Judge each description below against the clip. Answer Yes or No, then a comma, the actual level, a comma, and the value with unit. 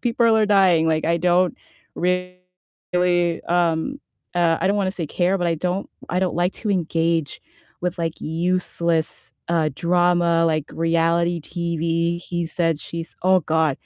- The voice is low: No, medium, 170 Hz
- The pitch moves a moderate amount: No, narrow, 1.7 semitones